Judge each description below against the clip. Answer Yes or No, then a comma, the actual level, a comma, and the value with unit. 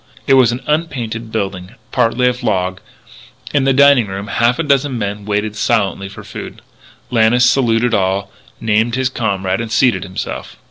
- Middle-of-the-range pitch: No, low, 115 Hz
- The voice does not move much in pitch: No, average, 3.9 semitones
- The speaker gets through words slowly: No, average, 160 wpm